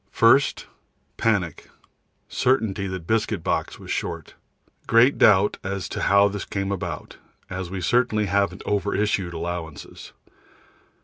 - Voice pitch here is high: No, low, 100 Hz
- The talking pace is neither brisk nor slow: No, slow, 130 wpm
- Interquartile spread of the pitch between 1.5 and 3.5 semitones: Yes, average, 2.9 semitones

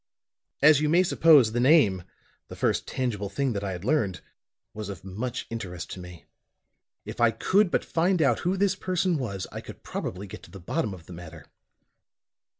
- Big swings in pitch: Yes, wide, 8.6 semitones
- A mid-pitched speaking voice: No, low, 115 Hz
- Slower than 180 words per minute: No, average, 190 wpm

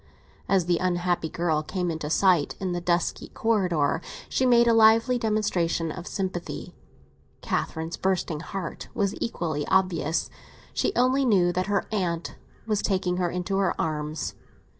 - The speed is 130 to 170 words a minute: Yes, average, 145 wpm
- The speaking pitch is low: No, medium, 180 Hz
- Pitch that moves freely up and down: No, average, 3.2 semitones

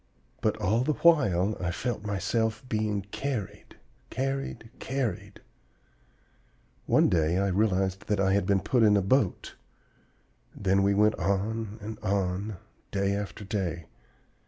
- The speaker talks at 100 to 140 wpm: Yes, slow, 135 wpm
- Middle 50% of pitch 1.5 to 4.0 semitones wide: Yes, narrow, 2.5 semitones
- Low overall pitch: Yes, low, 105 Hz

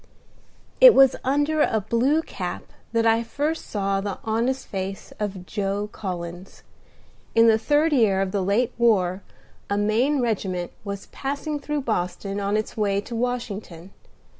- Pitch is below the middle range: No, high, 215 Hz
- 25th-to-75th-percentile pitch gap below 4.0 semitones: No, average, 4.4 semitones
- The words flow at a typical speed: Yes, average, 155 wpm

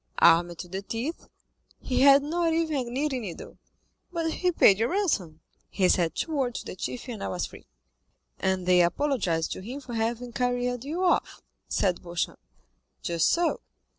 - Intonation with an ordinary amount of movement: No, wide, 8.0 semitones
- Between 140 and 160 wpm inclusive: No, average, 175 wpm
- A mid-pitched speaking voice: No, high, 245 Hz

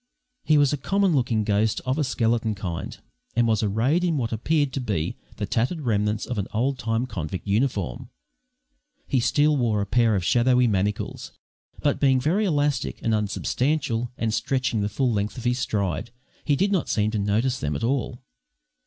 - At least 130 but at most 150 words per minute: No, average, 185 wpm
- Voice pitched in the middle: No, low, 120 Hz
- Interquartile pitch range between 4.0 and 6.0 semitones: Yes, average, 4.4 semitones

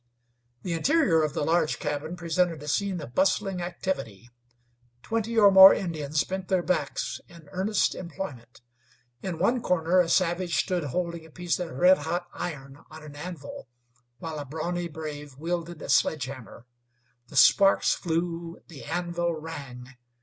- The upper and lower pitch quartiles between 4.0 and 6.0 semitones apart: No, average, 3.4 semitones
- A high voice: No, medium, 170 Hz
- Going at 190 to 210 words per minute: No, average, 155 wpm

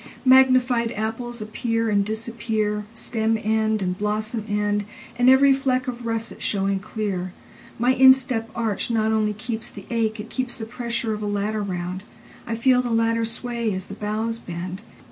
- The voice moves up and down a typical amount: No, narrow, 2.2 semitones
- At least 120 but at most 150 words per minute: Yes, average, 145 wpm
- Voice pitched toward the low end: No, high, 220 Hz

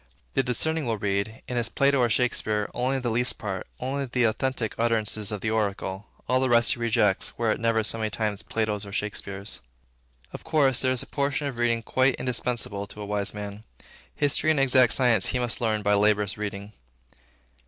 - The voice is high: No, low, 115 Hz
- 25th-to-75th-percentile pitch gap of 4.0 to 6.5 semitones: No, average, 3.3 semitones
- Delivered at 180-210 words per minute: Yes, average, 195 wpm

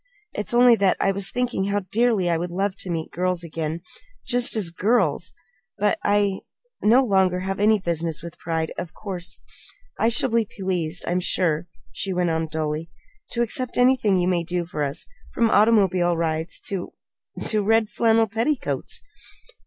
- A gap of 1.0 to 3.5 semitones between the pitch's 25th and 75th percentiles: No, average, 4.5 semitones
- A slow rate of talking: No, average, 170 wpm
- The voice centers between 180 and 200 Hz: Yes, high, 190 Hz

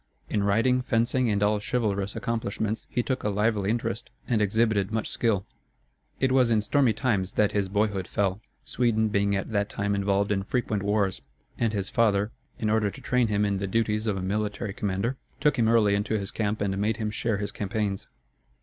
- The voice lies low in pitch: Yes, low, 105 Hz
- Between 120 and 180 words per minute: No, average, 195 wpm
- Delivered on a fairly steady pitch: Yes, narrow, 2.0 semitones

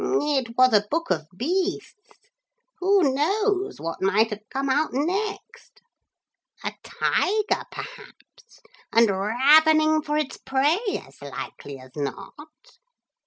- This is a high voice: Yes, very high, 295 Hz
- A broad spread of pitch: Yes, wide, 8.6 semitones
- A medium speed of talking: No, slow, 120 wpm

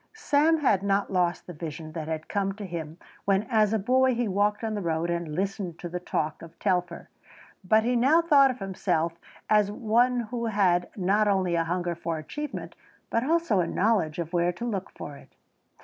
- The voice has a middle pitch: No, high, 195 Hz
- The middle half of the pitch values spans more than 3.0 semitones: Yes, average, 4.6 semitones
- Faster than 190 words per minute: Yes, average, 200 wpm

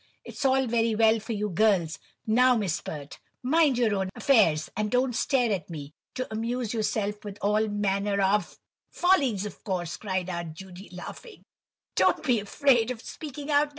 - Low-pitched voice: No, high, 215 Hz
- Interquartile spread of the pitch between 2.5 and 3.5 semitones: No, average, 4.5 semitones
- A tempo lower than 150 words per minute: No, average, 165 wpm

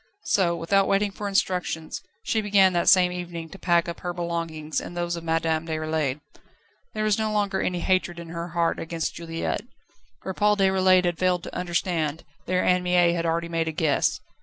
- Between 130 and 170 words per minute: No, average, 190 wpm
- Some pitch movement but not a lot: No, narrow, 2.2 semitones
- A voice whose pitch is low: No, medium, 175 Hz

